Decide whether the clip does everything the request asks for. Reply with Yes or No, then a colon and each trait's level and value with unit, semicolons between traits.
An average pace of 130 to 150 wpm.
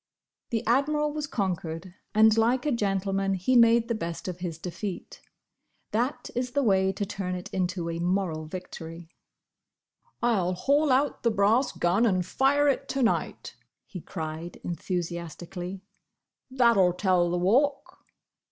Yes: average, 145 wpm